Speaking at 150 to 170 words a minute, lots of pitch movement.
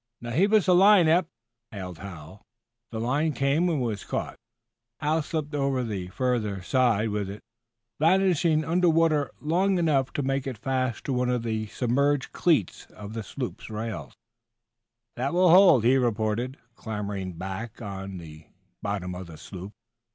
Yes: average, 165 wpm; wide, 6.9 semitones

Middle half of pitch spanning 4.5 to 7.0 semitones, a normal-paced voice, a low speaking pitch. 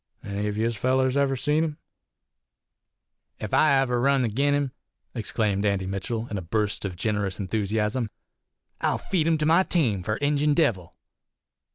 Yes: wide, 5.6 semitones; average, 160 wpm; low, 115 Hz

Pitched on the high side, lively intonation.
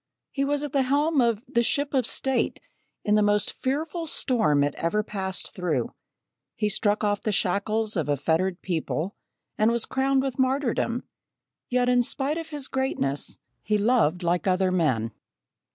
Yes: high, 220 Hz; wide, 6.4 semitones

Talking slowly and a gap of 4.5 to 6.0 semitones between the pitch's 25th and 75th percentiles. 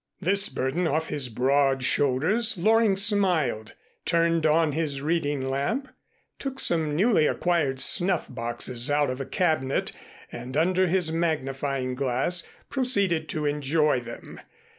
Yes: slow, 130 wpm; average, 4.9 semitones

